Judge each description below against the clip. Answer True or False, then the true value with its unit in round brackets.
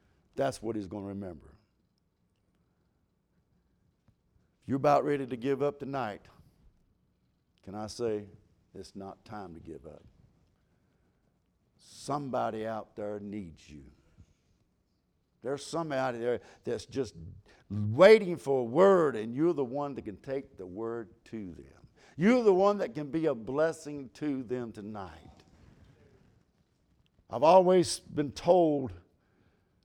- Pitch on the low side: True (115 Hz)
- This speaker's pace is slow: True (125 wpm)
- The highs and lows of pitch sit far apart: True (6.9 semitones)